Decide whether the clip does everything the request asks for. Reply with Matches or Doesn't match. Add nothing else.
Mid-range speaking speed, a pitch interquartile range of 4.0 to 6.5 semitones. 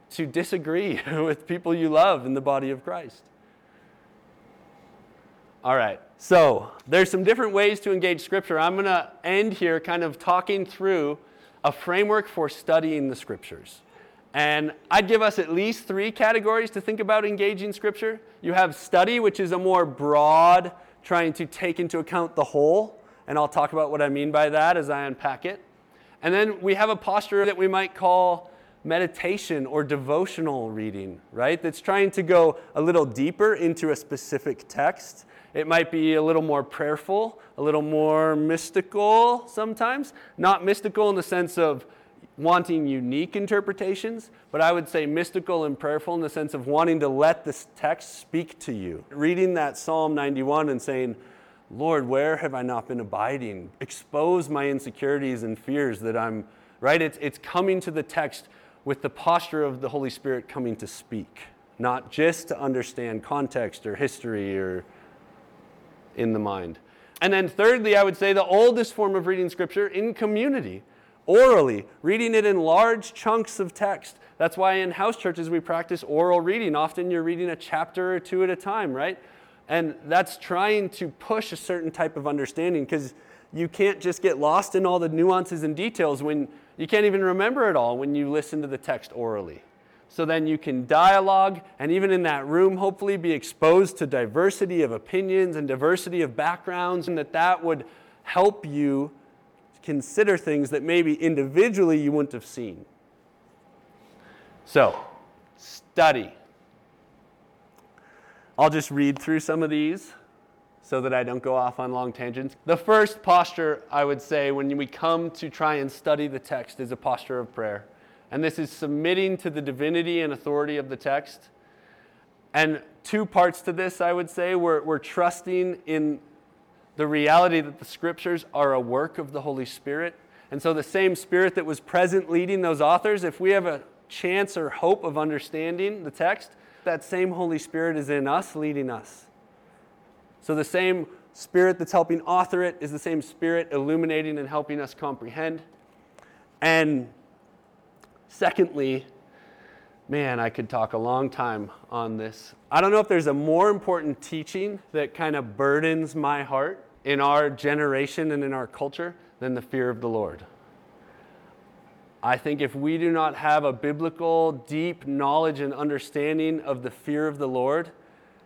Matches